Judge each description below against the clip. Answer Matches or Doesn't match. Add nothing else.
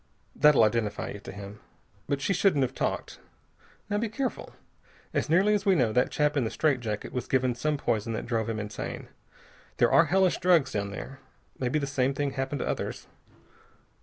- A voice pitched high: Doesn't match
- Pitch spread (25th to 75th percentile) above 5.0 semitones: Matches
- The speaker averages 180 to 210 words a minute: Matches